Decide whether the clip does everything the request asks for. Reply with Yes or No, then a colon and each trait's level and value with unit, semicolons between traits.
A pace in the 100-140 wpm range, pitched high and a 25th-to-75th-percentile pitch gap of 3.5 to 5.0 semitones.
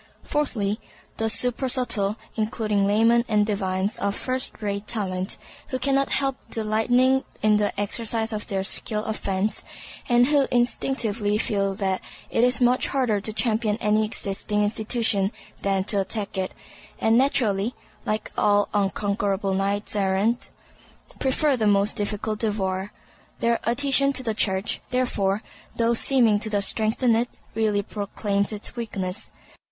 No: slow, 135 wpm; high, 215 Hz; average, 2.9 semitones